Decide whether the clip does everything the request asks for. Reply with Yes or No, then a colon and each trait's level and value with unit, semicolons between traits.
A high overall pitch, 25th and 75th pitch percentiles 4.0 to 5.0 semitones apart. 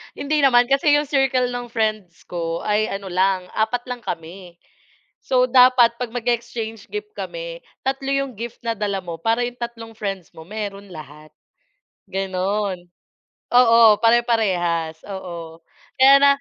Yes: high, 225 Hz; average, 4.7 semitones